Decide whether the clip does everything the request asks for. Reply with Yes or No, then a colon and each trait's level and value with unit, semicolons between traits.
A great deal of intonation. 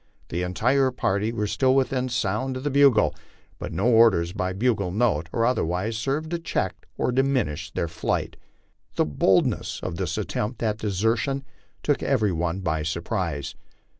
Yes: wide, 6.2 semitones